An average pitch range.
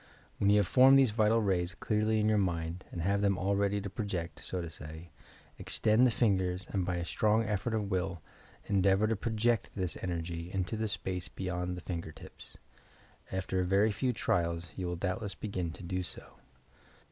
Yes: average, 3.1 semitones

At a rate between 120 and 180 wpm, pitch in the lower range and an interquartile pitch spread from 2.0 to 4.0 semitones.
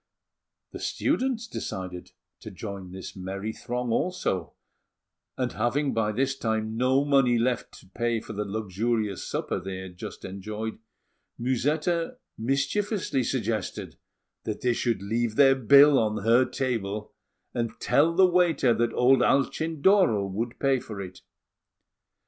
No: slow, 135 wpm; low, 120 Hz; average, 4.5 semitones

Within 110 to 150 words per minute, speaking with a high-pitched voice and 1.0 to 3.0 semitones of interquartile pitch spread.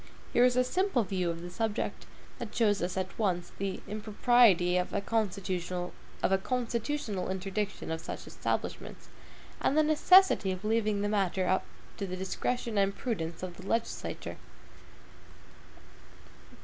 No: slow, 135 wpm; high, 200 Hz; average, 3.9 semitones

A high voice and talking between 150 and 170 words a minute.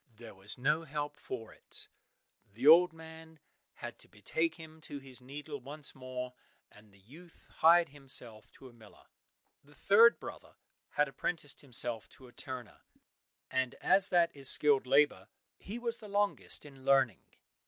No: medium, 140 Hz; average, 160 wpm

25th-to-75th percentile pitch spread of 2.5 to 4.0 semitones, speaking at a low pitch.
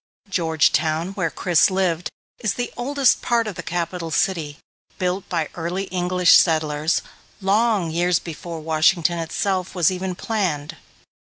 No: average, 2.8 semitones; medium, 175 Hz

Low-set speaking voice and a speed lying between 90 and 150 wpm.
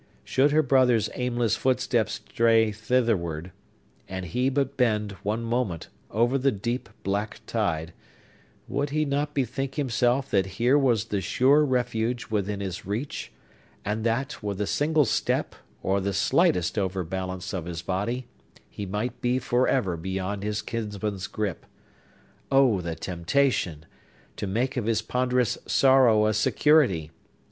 Yes: low, 110 Hz; average, 140 wpm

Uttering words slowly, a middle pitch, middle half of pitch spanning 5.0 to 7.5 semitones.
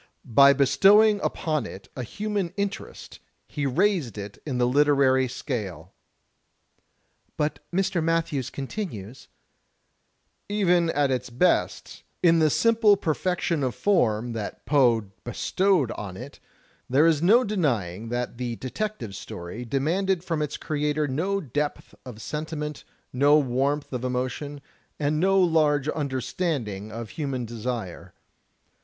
Yes: slow, 125 wpm; medium, 145 Hz; wide, 5.4 semitones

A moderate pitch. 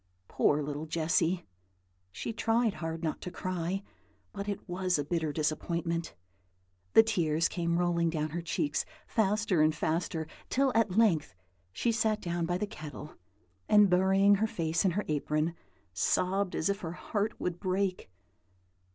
Yes: medium, 175 Hz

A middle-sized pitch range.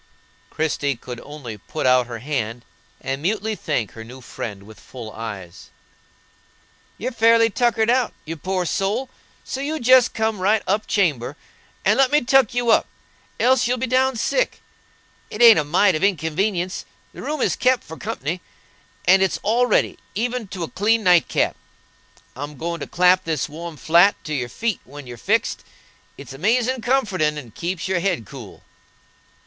No: wide, 8.0 semitones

